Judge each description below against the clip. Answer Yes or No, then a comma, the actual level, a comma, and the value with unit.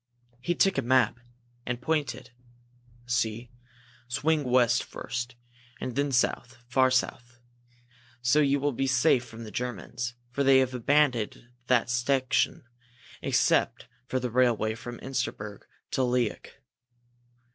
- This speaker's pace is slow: Yes, slow, 125 wpm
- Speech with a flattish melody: Yes, narrow, 1.7 semitones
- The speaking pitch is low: Yes, low, 125 Hz